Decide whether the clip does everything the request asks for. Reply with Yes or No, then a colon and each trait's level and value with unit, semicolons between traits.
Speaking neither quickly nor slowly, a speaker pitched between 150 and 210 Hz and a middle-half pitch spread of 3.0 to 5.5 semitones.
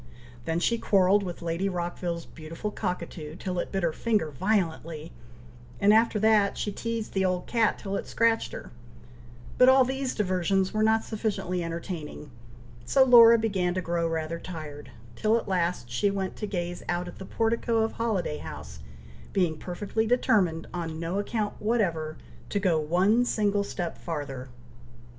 Yes: average, 160 wpm; medium, 185 Hz; average, 4.4 semitones